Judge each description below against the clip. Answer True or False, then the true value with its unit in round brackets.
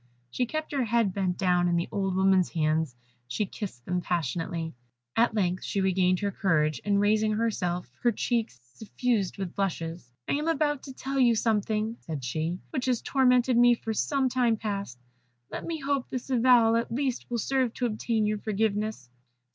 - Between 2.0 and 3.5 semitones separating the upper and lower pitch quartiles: False (5.2 semitones)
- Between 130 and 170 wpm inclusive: False (180 wpm)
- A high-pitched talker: True (215 Hz)